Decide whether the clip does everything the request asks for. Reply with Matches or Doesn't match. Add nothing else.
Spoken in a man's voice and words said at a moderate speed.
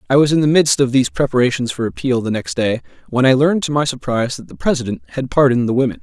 Doesn't match